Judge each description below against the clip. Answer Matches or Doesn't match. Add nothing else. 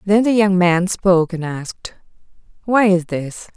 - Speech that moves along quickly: Doesn't match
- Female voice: Matches